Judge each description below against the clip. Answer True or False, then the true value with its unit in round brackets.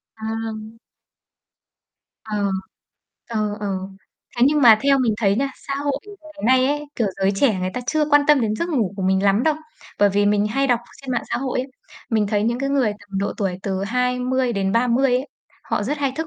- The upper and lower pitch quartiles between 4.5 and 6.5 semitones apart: True (4.9 semitones)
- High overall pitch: True (230 Hz)